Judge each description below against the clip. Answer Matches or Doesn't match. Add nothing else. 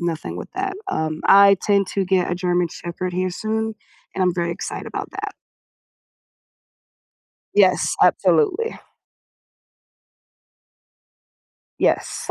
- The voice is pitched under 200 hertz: Matches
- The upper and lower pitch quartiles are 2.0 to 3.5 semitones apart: Matches